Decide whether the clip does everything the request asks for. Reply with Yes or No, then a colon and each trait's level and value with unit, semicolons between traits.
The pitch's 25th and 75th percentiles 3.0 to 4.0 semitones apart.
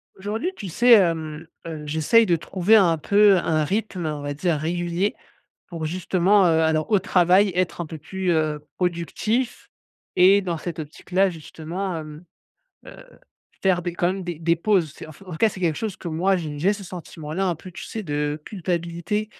Yes: average, 3.4 semitones